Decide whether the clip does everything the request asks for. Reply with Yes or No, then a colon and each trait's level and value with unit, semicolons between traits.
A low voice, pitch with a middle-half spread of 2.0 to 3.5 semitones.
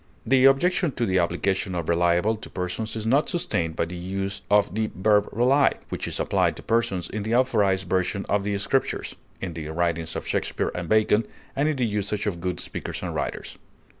No: low, 100 Hz; average, 4.2 semitones